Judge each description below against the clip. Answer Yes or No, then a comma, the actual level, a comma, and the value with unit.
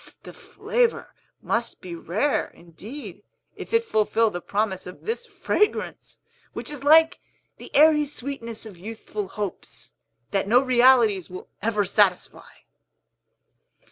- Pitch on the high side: Yes, high, 225 Hz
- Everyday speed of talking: No, slow, 125 wpm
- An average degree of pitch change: No, wide, 6.5 semitones